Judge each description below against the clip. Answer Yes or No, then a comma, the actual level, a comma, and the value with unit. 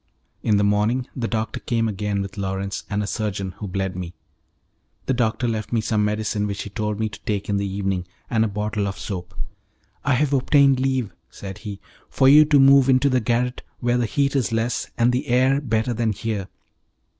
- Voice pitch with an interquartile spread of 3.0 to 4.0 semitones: Yes, average, 3.6 semitones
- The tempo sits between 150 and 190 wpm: No, fast, 205 wpm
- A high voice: No, low, 110 Hz